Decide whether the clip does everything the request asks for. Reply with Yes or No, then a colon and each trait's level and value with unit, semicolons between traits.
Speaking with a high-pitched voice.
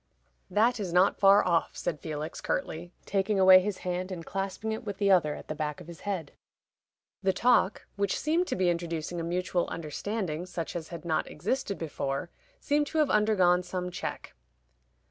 No: medium, 180 Hz